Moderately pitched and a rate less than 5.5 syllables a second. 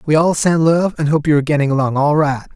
No: medium, 150 Hz; 6.4 syllables/s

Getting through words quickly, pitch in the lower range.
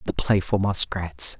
No: slow, 130 wpm; very low, 90 Hz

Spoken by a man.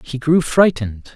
Yes: male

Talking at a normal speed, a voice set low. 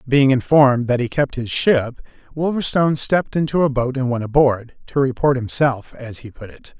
Yes: average, 195 wpm; low, 130 Hz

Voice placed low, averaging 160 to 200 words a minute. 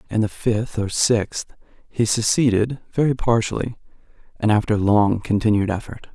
No: low, 110 Hz; slow, 135 wpm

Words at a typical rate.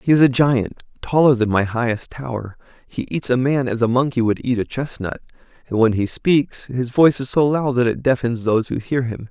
No: fast, 230 wpm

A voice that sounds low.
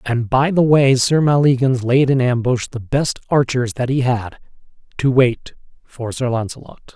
Yes: low, 130 Hz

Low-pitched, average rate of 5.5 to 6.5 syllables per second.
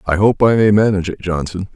Yes: very low, 95 Hz; 6.4 syllables/s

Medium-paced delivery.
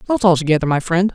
No: fast, 210 wpm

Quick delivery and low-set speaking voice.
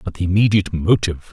No: average, 180 wpm; very low, 95 Hz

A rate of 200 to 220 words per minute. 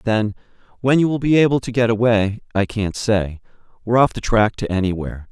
Yes: fast, 205 wpm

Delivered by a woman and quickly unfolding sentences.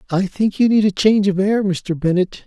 No: male; fast, 245 wpm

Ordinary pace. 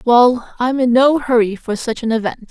No: fast, 215 wpm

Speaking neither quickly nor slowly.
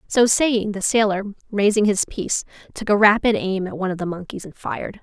No: fast, 215 wpm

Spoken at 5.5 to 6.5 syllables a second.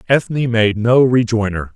No: 4.5 syllables/s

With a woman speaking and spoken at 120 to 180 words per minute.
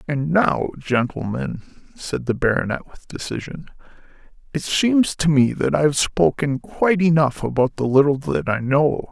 No: male; average, 160 wpm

